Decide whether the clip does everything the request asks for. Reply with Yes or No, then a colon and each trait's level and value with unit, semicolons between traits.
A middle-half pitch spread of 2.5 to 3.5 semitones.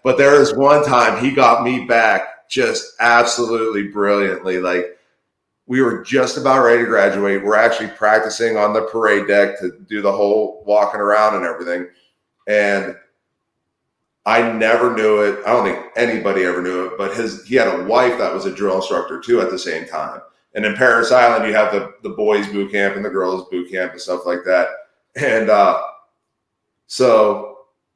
Yes: average, 3.1 semitones